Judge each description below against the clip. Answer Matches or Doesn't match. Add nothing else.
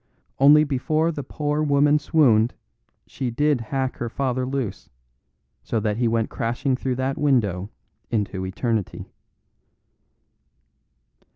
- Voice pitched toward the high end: Doesn't match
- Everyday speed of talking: Doesn't match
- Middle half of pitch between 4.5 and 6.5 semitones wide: Doesn't match